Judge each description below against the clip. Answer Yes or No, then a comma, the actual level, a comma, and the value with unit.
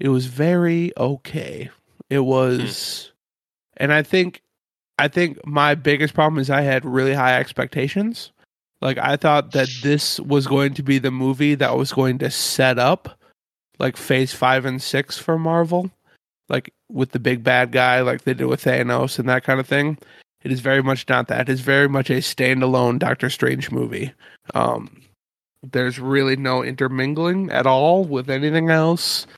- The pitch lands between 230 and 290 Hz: No, low, 135 Hz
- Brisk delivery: No, average, 175 wpm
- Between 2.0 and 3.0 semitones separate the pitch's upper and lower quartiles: Yes, average, 2.7 semitones